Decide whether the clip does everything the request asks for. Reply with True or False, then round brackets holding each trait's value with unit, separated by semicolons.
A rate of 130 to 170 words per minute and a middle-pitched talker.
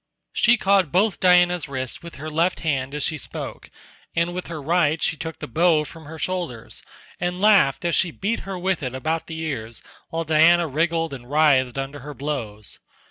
False (190 wpm; 160 Hz)